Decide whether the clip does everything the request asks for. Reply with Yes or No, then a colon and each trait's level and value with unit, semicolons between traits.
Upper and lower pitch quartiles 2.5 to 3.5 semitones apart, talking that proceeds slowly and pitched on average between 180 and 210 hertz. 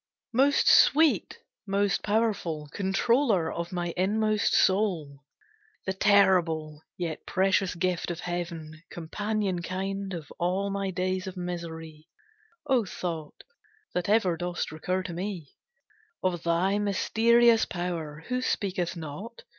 Yes: average, 3.2 semitones; slow, 120 wpm; medium, 185 Hz